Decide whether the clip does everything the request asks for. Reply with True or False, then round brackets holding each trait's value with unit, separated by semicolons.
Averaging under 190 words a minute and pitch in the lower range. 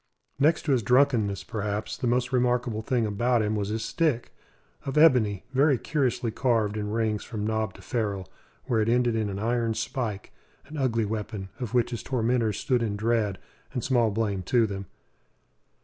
True (180 wpm; 115 Hz)